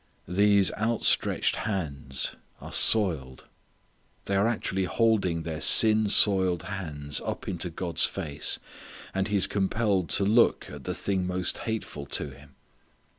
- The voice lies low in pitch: Yes, very low, 95 Hz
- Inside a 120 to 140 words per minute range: Yes, slow, 135 wpm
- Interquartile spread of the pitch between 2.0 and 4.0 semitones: No, average, 4.6 semitones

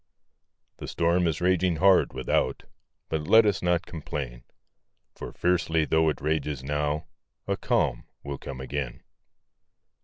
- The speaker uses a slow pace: Yes, slow, 130 wpm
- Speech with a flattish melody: No, average, 3.7 semitones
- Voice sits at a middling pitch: No, very low, 80 Hz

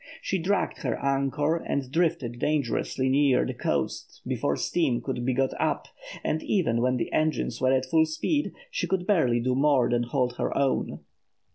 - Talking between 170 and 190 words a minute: Yes, average, 175 wpm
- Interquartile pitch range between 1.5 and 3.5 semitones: No, average, 4.0 semitones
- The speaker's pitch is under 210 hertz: Yes, low, 135 Hz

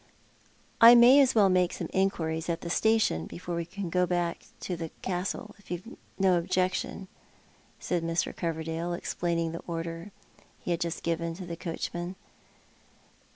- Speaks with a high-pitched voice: No, medium, 175 Hz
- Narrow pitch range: Yes, narrow, 2.1 semitones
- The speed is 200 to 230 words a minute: No, average, 155 wpm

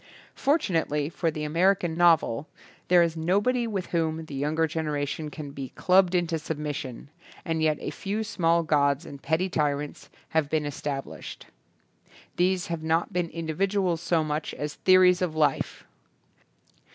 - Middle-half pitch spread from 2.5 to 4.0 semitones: Yes, average, 3.1 semitones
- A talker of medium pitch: Yes, medium, 160 Hz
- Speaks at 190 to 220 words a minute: No, average, 150 wpm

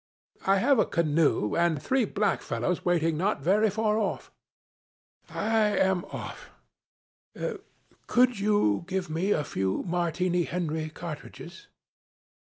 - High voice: No, medium, 180 Hz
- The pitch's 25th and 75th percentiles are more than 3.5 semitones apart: Yes, average, 4.3 semitones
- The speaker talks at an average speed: No, slow, 115 wpm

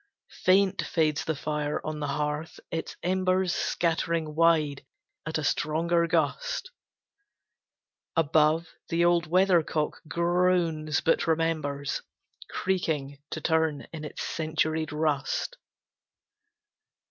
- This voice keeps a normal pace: No, slow, 100 wpm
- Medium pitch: Yes, medium, 160 Hz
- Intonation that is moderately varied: No, narrow, 2.0 semitones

